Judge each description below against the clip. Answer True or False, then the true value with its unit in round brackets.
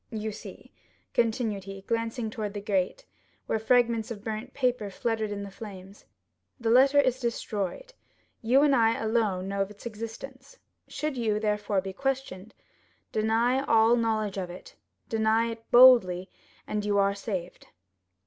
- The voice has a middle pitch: False (220 Hz)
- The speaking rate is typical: True (150 wpm)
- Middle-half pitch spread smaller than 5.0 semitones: True (2.9 semitones)